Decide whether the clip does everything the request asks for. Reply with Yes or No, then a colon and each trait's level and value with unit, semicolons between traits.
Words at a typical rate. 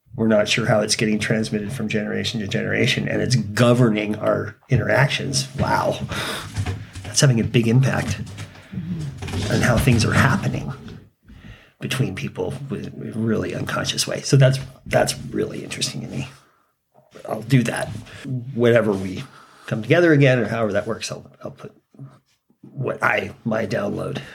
Yes: average, 150 wpm